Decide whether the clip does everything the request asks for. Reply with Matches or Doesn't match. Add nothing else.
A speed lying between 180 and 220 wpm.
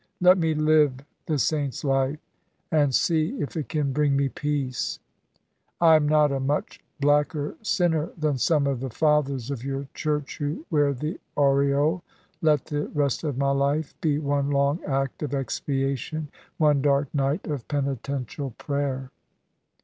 Doesn't match